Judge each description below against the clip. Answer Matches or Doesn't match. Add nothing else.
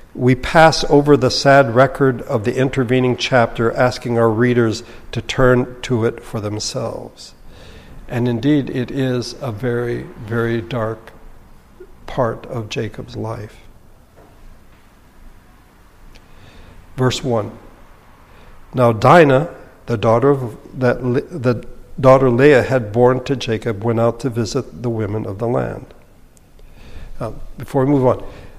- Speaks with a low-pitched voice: Matches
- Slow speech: Matches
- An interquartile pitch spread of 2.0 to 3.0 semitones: Matches